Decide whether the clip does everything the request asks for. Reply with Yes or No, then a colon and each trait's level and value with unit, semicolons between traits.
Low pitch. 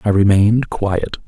Yes: low, 105 Hz